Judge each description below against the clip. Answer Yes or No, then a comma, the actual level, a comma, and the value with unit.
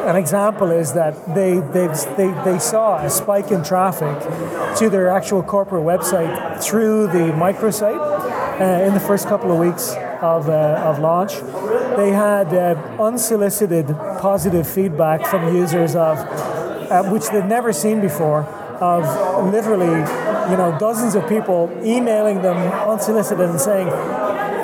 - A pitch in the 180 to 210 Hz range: Yes, high, 190 Hz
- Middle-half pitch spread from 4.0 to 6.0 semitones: No, average, 3.4 semitones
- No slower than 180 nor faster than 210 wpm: No, average, 145 wpm